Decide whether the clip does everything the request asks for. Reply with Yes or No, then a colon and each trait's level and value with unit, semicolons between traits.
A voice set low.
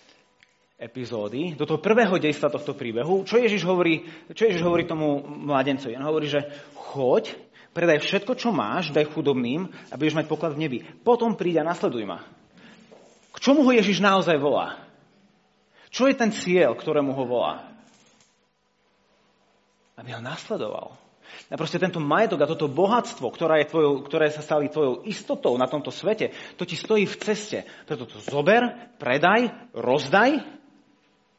No: medium, 170 Hz